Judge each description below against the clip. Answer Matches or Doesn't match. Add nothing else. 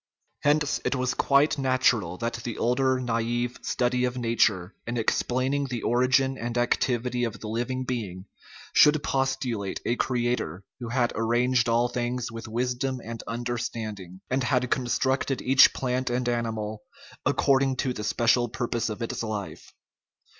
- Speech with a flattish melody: Matches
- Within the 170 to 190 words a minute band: Doesn't match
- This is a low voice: Matches